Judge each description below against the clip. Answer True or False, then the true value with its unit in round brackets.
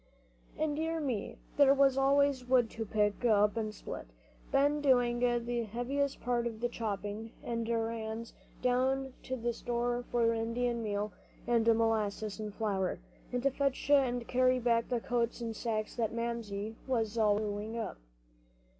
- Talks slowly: False (155 wpm)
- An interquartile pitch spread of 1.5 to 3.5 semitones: True (2.4 semitones)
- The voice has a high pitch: True (235 Hz)